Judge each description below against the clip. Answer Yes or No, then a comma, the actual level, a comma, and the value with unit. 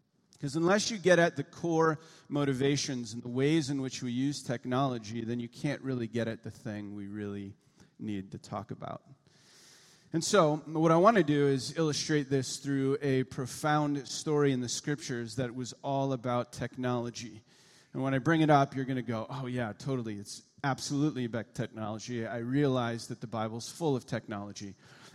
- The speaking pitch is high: No, low, 135 Hz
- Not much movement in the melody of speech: No, average, 3.8 semitones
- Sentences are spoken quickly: No, average, 185 wpm